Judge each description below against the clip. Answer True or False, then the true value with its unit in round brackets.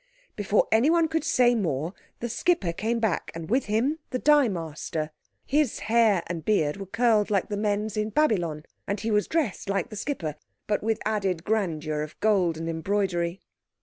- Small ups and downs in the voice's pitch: False (5.1 semitones)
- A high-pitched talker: True (205 Hz)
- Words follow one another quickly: False (180 wpm)